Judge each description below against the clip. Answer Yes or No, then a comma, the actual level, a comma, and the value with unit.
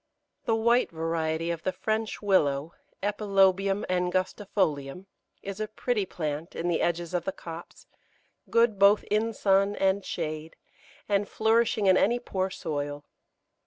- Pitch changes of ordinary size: Yes, average, 3.9 semitones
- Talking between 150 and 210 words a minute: No, slow, 135 wpm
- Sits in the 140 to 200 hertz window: Yes, high, 190 Hz